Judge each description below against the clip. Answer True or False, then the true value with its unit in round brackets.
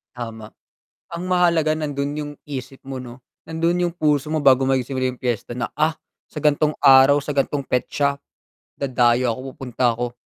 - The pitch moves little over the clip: False (3.2 semitones)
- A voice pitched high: False (140 Hz)